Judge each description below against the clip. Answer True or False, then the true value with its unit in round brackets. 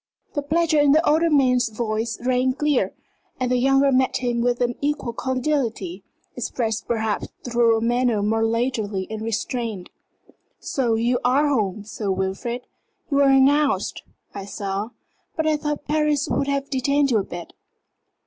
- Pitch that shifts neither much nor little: True (4.0 semitones)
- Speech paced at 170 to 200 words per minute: False (160 wpm)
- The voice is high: True (245 Hz)